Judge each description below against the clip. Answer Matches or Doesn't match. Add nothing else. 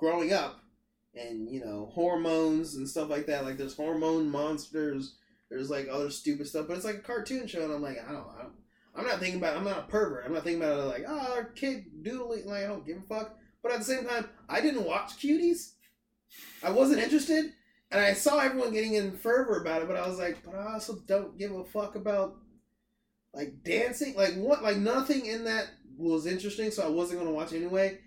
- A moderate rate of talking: Doesn't match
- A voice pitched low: Doesn't match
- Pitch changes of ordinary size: Doesn't match